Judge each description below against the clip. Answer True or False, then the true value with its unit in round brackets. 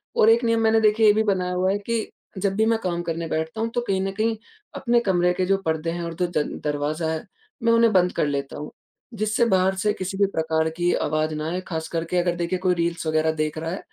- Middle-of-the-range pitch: True (180 Hz)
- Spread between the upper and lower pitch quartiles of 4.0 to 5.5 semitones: True (4.8 semitones)